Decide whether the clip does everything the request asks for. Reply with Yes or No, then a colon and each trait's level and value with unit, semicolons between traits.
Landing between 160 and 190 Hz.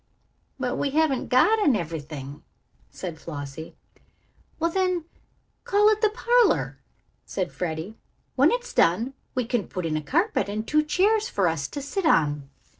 No: high, 245 Hz